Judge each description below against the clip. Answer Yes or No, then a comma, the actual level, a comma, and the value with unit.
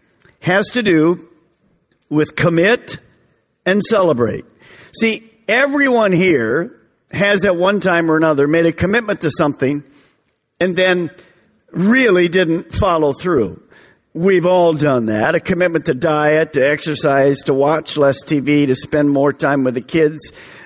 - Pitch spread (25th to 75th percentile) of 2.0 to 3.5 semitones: No, average, 4.0 semitones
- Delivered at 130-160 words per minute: Yes, average, 140 wpm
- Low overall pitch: No, medium, 165 Hz